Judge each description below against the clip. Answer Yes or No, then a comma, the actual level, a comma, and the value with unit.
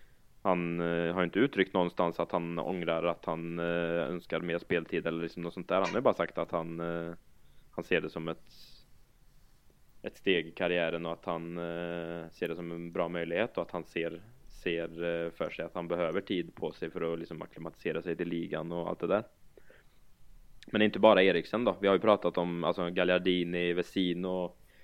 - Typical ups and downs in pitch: No, narrow, 1.1 semitones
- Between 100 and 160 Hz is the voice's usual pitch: No, very low, 85 Hz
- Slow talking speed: No, average, 190 wpm